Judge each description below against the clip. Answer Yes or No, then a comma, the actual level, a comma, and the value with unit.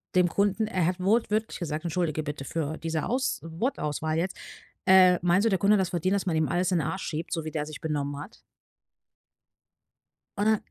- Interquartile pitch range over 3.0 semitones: Yes, average, 3.7 semitones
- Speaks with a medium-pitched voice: Yes, medium, 175 Hz